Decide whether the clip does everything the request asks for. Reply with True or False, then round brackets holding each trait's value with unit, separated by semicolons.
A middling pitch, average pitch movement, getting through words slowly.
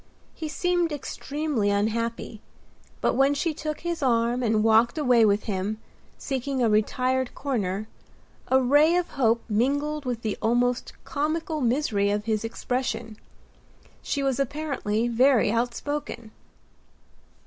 False (245 Hz; 4.4 semitones; 125 wpm)